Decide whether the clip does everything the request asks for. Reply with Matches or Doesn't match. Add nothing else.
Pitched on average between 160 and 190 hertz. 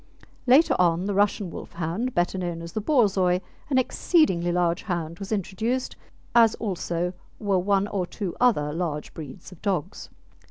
Matches